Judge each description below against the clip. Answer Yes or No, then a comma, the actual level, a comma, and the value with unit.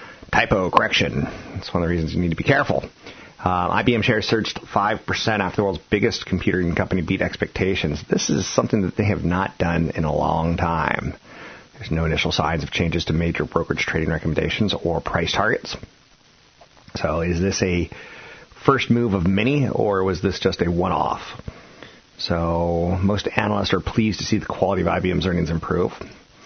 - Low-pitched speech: Yes, very low, 95 Hz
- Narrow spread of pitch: No, average, 3.2 semitones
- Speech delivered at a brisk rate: No, average, 175 wpm